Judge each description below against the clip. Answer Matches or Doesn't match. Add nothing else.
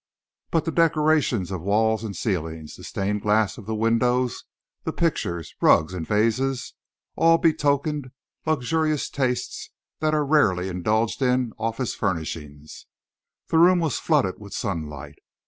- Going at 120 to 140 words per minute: Matches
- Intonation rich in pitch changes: Matches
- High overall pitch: Doesn't match